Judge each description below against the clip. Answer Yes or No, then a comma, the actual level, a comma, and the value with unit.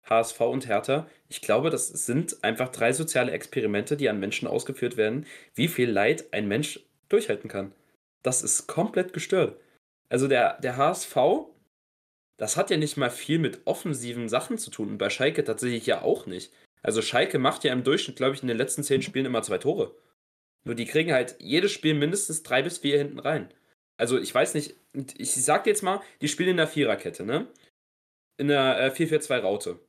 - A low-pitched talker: No, medium, 145 Hz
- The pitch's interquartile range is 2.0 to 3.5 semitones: No, average, 4.5 semitones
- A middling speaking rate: No, fast, 195 wpm